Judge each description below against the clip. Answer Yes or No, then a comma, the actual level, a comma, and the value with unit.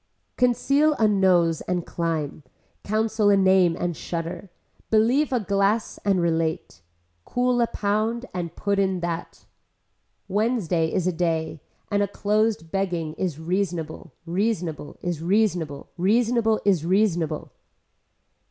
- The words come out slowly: Yes, slow, 125 wpm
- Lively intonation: No, average, 4.4 semitones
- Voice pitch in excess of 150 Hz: Yes, high, 190 Hz